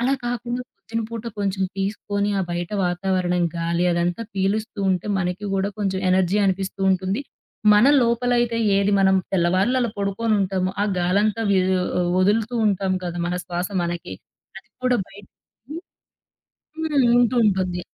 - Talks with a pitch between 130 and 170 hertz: No, high, 195 Hz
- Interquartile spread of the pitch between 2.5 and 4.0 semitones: Yes, average, 3.0 semitones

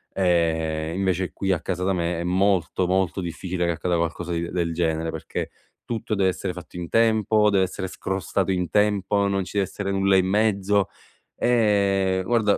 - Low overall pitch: Yes, very low, 95 Hz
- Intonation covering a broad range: No, narrow, 2.4 semitones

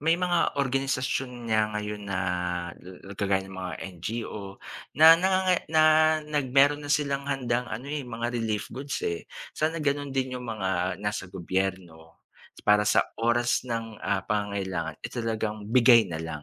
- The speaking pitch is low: Yes, low, 115 Hz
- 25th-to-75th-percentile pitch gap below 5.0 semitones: No, wide, 5.4 semitones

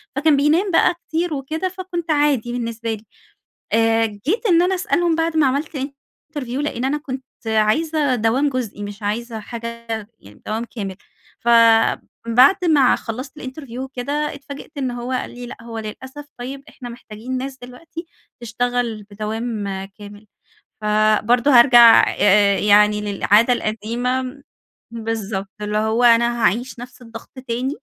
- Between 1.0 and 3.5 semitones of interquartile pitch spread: No, average, 4.1 semitones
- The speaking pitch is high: Yes, high, 245 Hz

